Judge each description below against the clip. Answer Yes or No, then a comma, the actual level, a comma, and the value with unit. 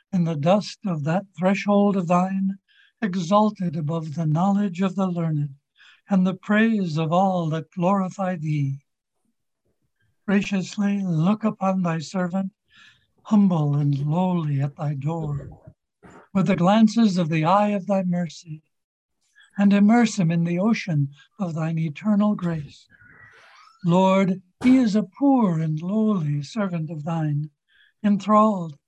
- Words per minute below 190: Yes, slow, 135 wpm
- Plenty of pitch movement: No, average, 3.8 semitones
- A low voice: No, medium, 185 Hz